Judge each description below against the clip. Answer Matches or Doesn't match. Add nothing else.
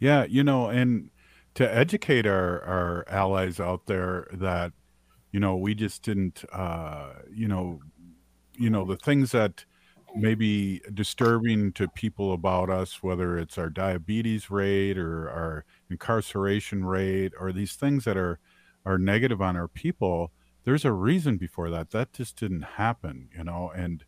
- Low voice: Matches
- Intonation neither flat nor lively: Matches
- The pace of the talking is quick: Doesn't match